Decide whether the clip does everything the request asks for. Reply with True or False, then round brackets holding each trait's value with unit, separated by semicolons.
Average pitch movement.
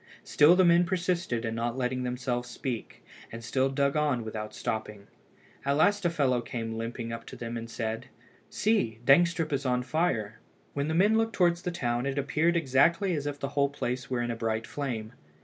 False (5.8 semitones)